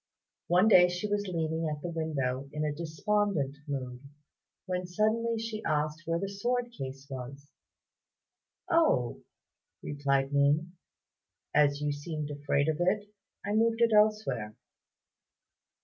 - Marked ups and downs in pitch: Yes, wide, 6.4 semitones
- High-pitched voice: No, medium, 160 Hz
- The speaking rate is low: Yes, slow, 130 wpm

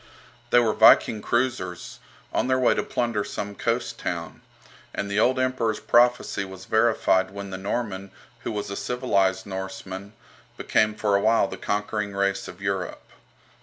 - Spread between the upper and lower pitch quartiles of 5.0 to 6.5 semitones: No, average, 3.2 semitones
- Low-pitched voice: Yes, low, 100 Hz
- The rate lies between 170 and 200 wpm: No, average, 160 wpm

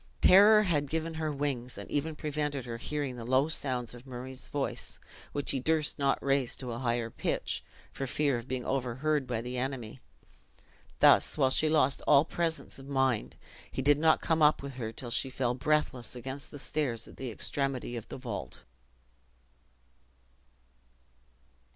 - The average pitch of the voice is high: No, low, 135 Hz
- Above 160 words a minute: Yes, average, 170 wpm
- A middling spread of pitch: Yes, average, 3.2 semitones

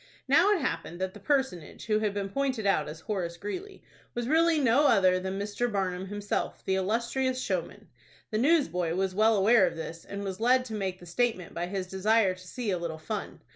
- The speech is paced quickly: Yes, fast, 210 wpm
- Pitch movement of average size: Yes, average, 4.7 semitones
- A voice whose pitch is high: Yes, high, 205 Hz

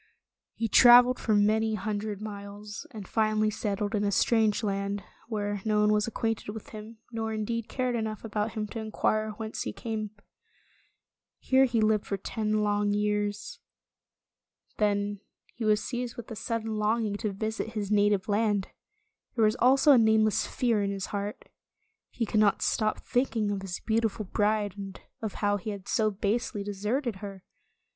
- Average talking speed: Yes, average, 170 wpm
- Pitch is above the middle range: Yes, high, 215 Hz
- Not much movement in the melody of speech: Yes, narrow, 1.5 semitones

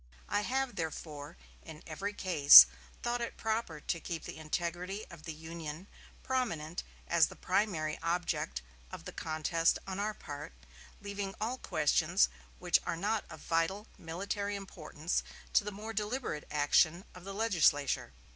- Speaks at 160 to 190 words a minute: No, average, 145 wpm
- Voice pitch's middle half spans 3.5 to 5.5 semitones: Yes, average, 4.6 semitones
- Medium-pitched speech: Yes, medium, 175 Hz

